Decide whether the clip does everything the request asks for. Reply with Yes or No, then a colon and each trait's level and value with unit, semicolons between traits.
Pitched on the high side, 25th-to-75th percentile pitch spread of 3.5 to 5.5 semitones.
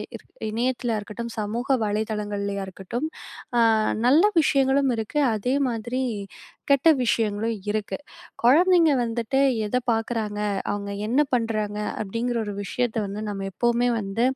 No: high, 230 Hz; average, 3.1 semitones